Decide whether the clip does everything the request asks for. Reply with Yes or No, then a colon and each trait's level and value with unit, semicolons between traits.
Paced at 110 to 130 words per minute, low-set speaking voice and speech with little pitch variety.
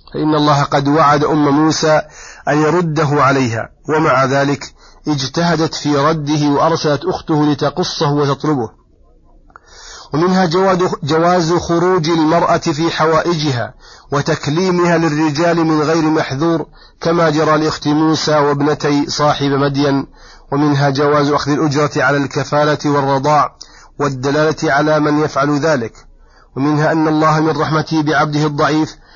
No: average, 115 wpm; medium, 150 Hz; narrow, 1.7 semitones